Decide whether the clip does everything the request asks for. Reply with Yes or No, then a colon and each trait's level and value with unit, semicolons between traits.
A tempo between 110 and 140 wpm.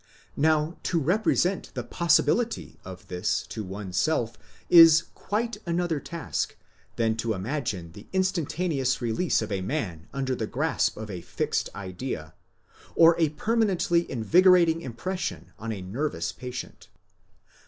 Yes: slow, 135 wpm